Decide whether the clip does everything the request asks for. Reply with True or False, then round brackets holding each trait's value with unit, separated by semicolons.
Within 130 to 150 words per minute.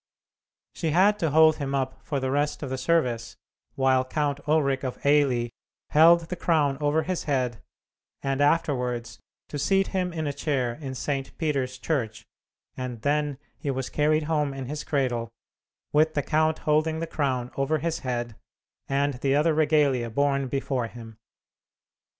False (160 wpm)